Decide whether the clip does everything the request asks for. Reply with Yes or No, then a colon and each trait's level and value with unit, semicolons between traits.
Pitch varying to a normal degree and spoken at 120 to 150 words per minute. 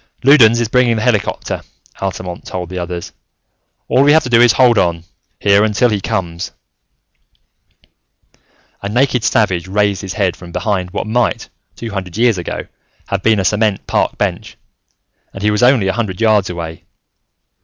No: average, 4.0 semitones; average, 170 wpm